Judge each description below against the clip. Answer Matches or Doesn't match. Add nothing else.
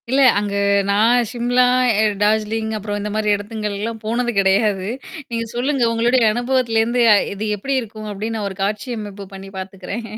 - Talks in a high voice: Matches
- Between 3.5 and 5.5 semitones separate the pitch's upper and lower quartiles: Doesn't match